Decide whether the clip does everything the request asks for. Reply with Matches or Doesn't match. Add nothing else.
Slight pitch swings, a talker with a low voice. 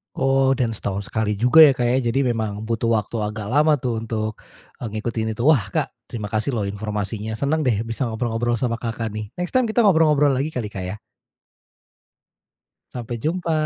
Doesn't match